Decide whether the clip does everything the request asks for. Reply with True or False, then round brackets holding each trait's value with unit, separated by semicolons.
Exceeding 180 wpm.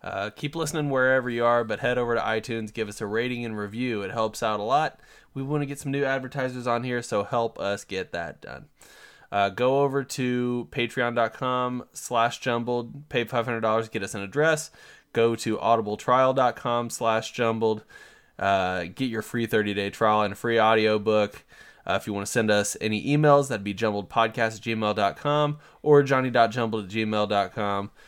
False (170 wpm)